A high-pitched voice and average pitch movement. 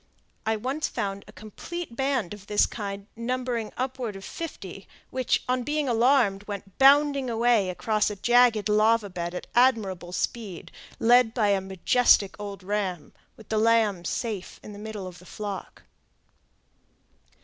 Yes: high, 215 Hz; average, 3.7 semitones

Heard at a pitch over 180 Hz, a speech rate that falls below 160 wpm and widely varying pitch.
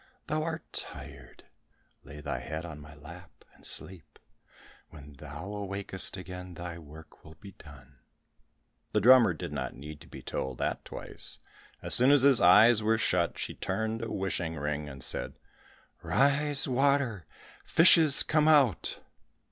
No: very low, 90 Hz; average, 150 wpm; wide, 8.6 semitones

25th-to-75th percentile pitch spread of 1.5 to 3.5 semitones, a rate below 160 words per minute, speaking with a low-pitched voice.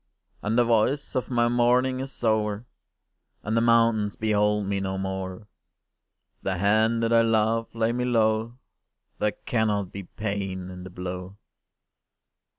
Yes: average, 2.8 semitones; average, 150 wpm; low, 110 Hz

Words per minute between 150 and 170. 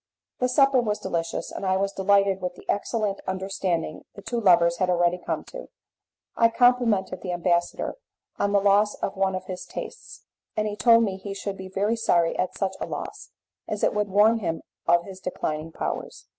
No: average, 195 wpm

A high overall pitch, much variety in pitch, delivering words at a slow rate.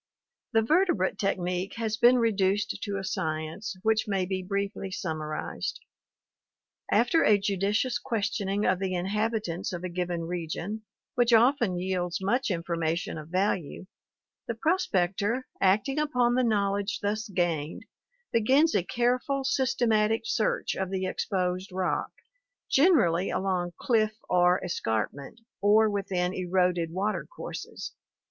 No: high, 200 Hz; average, 3.8 semitones; slow, 125 wpm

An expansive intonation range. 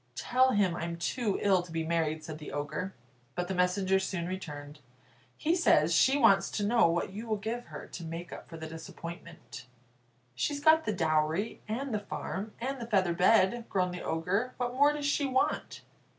Yes: wide, 5.9 semitones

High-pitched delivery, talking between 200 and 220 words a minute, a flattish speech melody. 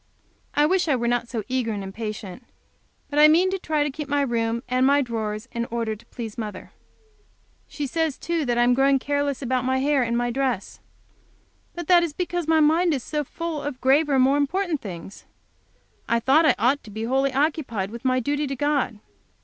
No: very high, 265 Hz; fast, 205 wpm; average, 4.1 semitones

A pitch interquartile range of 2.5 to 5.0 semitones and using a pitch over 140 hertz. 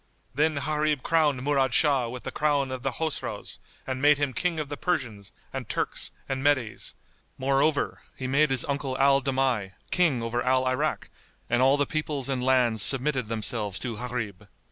No: average, 2.8 semitones; low, 135 Hz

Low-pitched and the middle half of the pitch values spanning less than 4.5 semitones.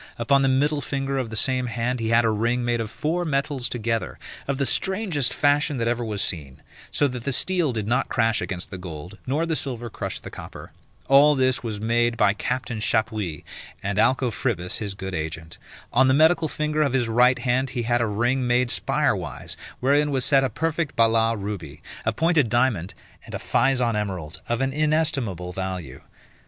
Yes: low, 120 Hz; average, 4.1 semitones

